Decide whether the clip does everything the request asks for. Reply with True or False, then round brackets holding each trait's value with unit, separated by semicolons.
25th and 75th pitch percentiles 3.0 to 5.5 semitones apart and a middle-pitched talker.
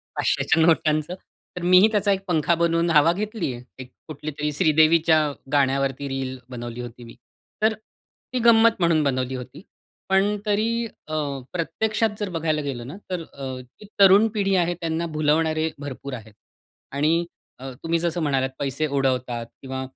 True (4.7 semitones; 155 Hz)